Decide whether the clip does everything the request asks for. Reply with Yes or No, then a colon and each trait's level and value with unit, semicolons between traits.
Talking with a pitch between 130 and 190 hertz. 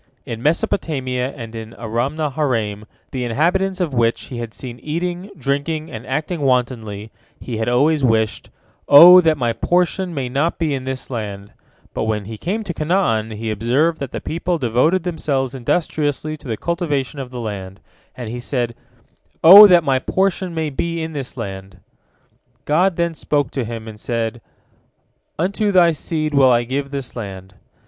Yes: low, 135 Hz